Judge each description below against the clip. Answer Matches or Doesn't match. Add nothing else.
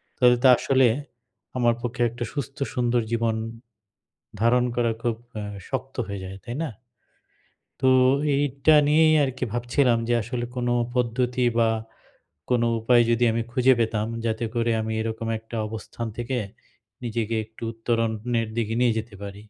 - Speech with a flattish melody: Matches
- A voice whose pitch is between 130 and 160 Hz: Doesn't match